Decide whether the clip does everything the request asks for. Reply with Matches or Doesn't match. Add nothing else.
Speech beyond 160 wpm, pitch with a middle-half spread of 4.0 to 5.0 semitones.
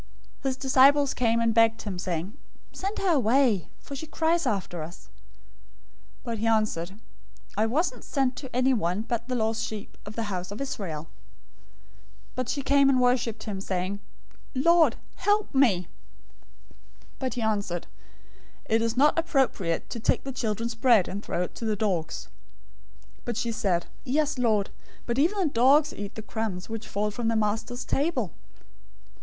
Matches